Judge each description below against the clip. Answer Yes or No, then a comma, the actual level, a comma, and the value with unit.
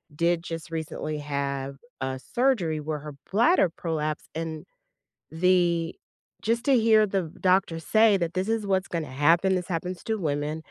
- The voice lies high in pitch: No, medium, 170 Hz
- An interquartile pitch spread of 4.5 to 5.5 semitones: No, average, 3.8 semitones